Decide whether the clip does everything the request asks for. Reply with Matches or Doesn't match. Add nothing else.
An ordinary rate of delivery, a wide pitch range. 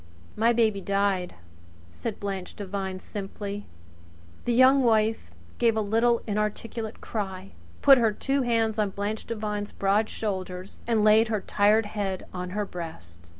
Doesn't match